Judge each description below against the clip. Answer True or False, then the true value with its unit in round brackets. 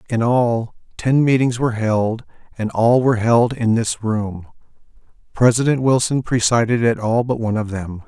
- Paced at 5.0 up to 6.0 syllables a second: False (4.8 syllables/s)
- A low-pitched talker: True (115 Hz)